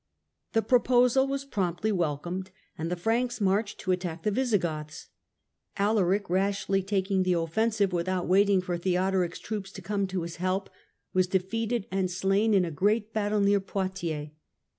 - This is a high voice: Yes, high, 195 Hz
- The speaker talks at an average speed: Yes, average, 160 wpm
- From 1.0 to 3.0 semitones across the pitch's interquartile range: Yes, average, 2.7 semitones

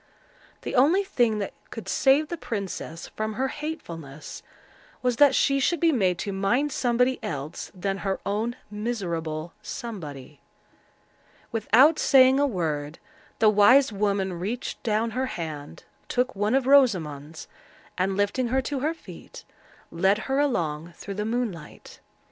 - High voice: Yes, high, 215 Hz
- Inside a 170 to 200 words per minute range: No, average, 140 wpm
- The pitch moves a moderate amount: No, wide, 6.8 semitones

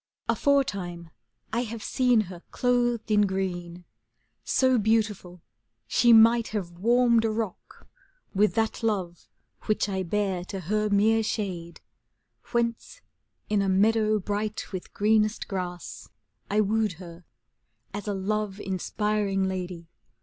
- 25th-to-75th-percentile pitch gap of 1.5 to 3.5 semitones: Yes, average, 2.9 semitones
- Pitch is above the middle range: Yes, high, 210 Hz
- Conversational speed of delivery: No, slow, 130 wpm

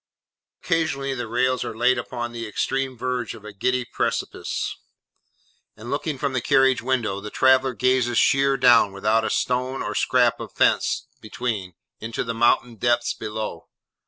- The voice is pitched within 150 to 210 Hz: No, low, 120 Hz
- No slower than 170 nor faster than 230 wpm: No, average, 160 wpm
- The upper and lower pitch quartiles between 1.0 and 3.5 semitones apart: Yes, narrow, 2.5 semitones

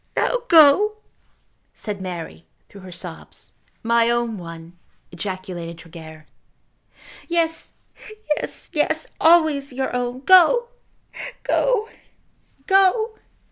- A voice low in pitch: No, high, 240 Hz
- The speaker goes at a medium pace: No, slow, 95 wpm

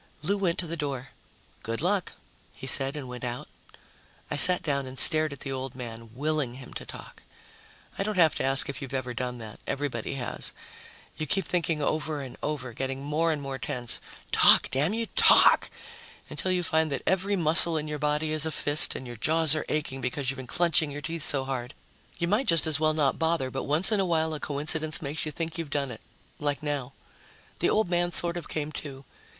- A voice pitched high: No, medium, 150 Hz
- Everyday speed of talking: No, fast, 215 wpm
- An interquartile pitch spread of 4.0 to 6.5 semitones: No, average, 3.4 semitones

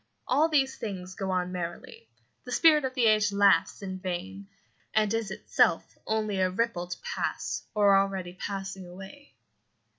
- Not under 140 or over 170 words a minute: Yes, average, 155 wpm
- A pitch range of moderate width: Yes, average, 3.4 semitones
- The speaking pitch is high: Yes, high, 195 Hz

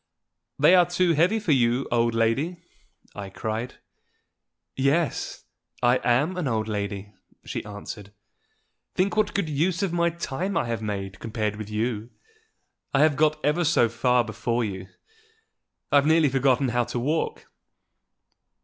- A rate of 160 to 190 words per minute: No, average, 145 wpm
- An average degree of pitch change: No, wide, 6.4 semitones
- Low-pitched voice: Yes, low, 125 Hz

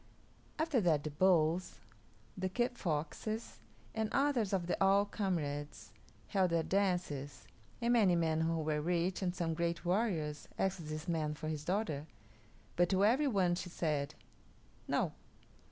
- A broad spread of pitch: No, average, 3.9 semitones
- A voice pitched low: No, medium, 175 Hz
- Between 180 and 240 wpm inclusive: No, average, 150 wpm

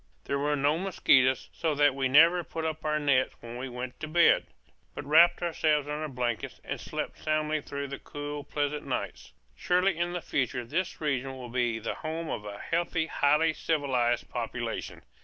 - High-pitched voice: No, medium, 145 Hz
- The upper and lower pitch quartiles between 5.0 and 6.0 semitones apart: No, average, 3.5 semitones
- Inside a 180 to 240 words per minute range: Yes, average, 185 wpm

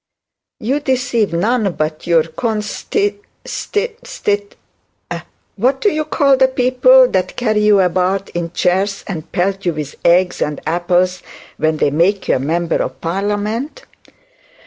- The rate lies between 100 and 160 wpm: Yes, average, 145 wpm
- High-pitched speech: Yes, high, 200 Hz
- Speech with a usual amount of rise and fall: No, wide, 6.5 semitones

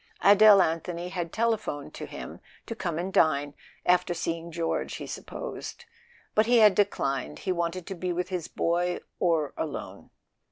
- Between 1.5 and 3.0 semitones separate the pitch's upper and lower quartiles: Yes, average, 2.7 semitones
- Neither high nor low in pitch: Yes, medium, 175 Hz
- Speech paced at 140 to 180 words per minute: Yes, average, 155 wpm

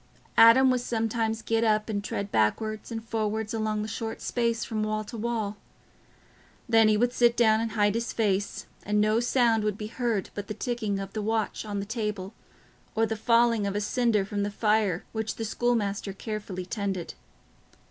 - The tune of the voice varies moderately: No, narrow, 1.8 semitones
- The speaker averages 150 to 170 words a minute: No, average, 190 wpm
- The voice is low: No, high, 220 Hz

